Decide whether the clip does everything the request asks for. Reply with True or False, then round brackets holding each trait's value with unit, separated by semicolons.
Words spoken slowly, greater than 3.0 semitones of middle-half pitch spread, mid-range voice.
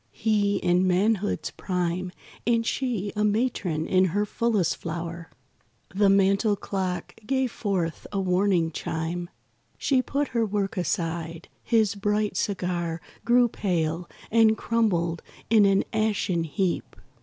False (125 wpm; 3.7 semitones; 195 Hz)